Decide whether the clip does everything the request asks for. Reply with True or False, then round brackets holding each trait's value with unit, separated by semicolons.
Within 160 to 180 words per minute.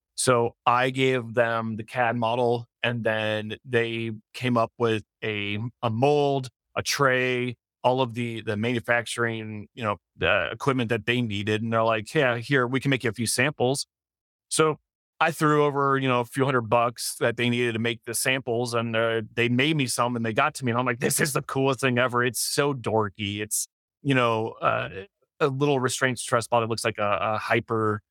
False (205 wpm)